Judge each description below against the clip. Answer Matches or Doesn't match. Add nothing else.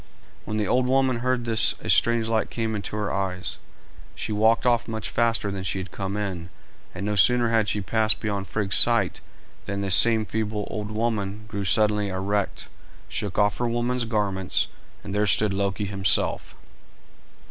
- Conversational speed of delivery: Matches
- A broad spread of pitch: Doesn't match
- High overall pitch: Doesn't match